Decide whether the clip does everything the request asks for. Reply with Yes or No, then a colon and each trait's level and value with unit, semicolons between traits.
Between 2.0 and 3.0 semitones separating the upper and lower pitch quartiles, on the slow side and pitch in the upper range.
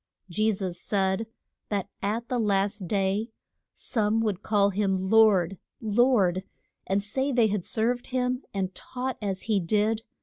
No: average, 2.7 semitones; average, 145 wpm; high, 210 Hz